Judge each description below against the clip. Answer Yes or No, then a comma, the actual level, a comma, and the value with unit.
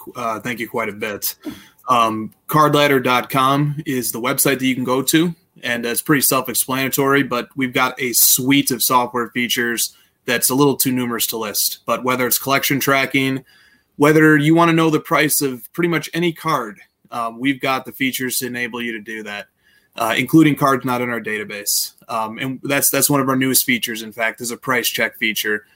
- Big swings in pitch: No, average, 2.9 semitones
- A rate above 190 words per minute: Yes, average, 200 wpm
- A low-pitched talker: Yes, low, 130 Hz